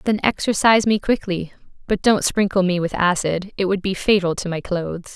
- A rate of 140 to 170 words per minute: No, average, 200 wpm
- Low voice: No, high, 190 Hz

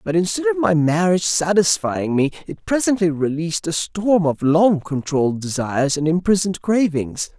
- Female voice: No, male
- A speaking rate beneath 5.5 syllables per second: Yes, 5.2 syllables/s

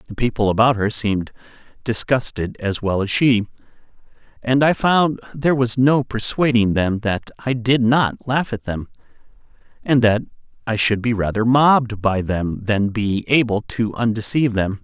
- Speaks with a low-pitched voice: Yes, low, 115 Hz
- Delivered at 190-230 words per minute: No, average, 160 wpm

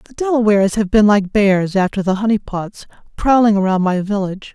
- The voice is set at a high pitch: Yes, high, 205 Hz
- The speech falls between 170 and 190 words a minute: Yes, average, 185 wpm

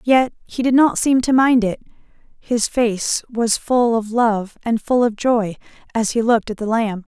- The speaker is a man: No, female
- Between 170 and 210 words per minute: Yes, average, 200 wpm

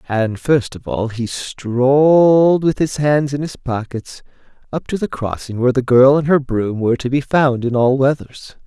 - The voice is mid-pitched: No, low, 130 Hz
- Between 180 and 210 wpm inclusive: Yes, average, 200 wpm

